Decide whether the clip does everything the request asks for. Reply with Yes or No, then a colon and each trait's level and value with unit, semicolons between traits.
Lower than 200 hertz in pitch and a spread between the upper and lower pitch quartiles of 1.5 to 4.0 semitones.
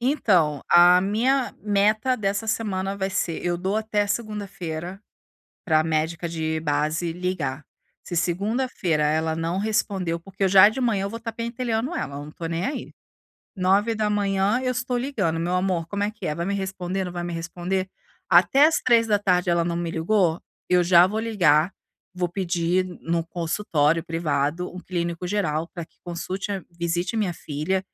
Yes: medium, 185 Hz; average, 3.7 semitones